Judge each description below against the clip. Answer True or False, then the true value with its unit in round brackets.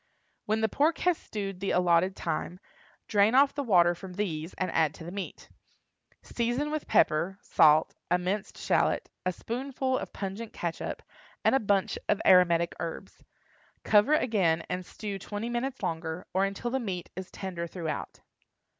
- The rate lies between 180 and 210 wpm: False (165 wpm)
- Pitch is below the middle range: False (195 Hz)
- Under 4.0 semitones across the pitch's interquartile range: False (4.9 semitones)